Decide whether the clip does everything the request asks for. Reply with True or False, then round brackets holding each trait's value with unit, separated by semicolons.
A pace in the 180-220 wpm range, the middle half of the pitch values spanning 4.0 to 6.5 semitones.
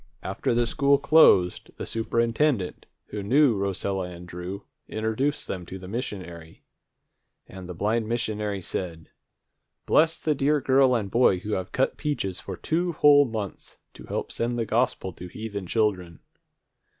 False (150 wpm; 5.5 semitones)